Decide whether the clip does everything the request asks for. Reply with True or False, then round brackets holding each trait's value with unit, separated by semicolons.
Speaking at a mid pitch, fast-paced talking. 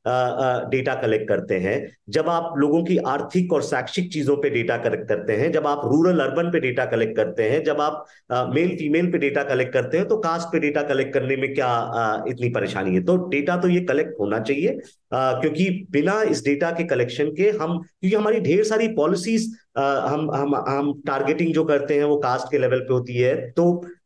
True (150 Hz; 220 wpm)